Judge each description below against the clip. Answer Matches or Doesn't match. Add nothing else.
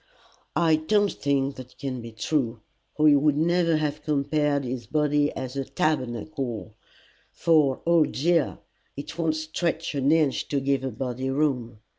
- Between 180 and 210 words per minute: Doesn't match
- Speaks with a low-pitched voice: Doesn't match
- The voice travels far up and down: Doesn't match